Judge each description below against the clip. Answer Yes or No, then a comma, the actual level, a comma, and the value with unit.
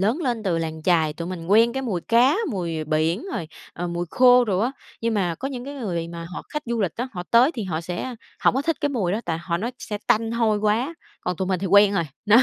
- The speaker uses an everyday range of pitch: No, wide, 5.7 semitones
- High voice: Yes, high, 205 Hz